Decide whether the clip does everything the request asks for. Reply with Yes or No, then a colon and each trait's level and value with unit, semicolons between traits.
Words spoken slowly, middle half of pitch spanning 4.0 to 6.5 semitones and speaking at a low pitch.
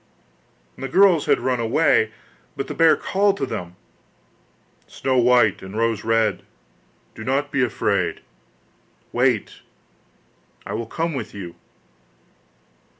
Yes: slow, 120 wpm; average, 4.7 semitones; low, 125 Hz